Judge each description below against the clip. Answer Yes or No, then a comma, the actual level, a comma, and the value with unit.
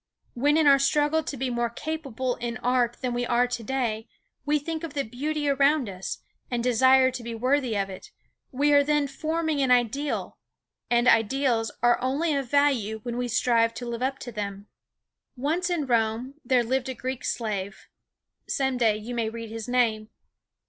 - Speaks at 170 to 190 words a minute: Yes, average, 185 wpm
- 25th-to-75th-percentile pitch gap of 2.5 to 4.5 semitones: Yes, average, 3.4 semitones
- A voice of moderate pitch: No, very high, 250 Hz